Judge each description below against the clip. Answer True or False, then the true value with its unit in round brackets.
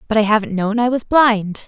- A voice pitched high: True (220 Hz)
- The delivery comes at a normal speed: False (250 wpm)